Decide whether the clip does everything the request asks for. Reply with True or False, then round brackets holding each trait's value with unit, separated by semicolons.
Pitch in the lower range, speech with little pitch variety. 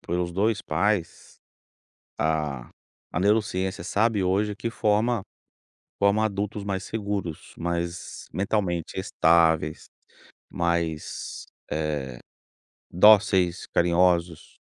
False (90 Hz; 3.5 semitones)